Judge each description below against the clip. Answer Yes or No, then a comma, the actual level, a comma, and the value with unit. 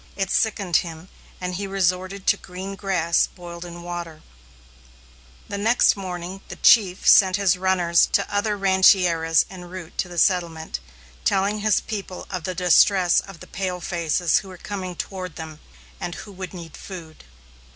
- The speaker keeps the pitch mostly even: Yes, narrow, 2.1 semitones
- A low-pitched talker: No, medium, 185 Hz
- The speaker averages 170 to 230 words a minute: No, average, 160 wpm